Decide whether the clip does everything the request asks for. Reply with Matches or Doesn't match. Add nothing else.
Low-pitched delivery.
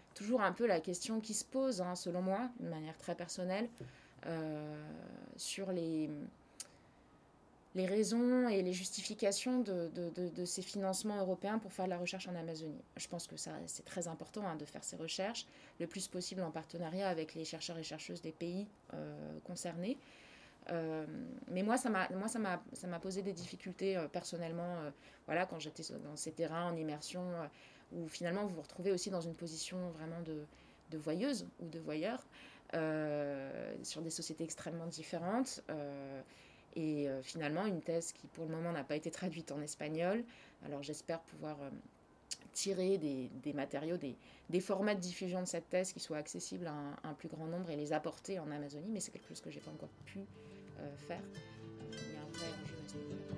Doesn't match